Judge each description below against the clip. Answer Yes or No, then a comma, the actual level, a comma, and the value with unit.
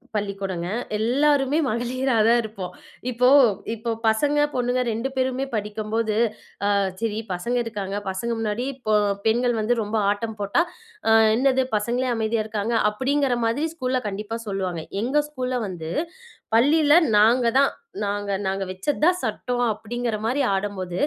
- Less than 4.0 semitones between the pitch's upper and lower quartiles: Yes, average, 3.6 semitones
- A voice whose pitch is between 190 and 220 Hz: No, high, 230 Hz